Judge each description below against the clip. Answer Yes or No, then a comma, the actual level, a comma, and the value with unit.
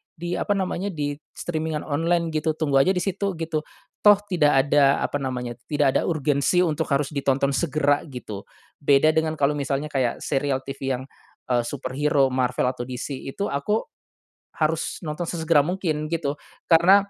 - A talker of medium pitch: Yes, medium, 150 Hz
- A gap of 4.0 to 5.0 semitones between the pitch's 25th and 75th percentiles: No, average, 3.3 semitones